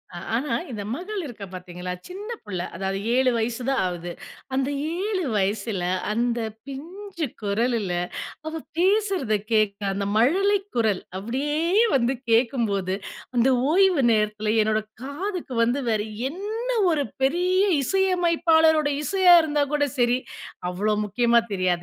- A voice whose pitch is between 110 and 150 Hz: No, very high, 255 Hz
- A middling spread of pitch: No, wide, 8.2 semitones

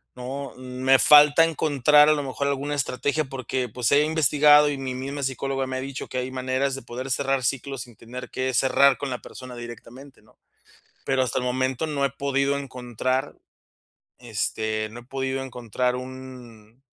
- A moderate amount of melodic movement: No, narrow, 1.8 semitones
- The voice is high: No, low, 130 Hz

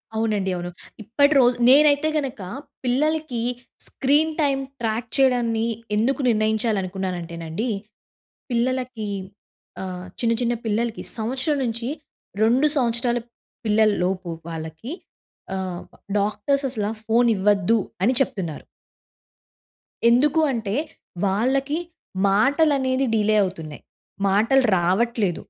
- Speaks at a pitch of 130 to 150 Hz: No, high, 230 Hz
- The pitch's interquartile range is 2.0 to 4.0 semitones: No, average, 4.8 semitones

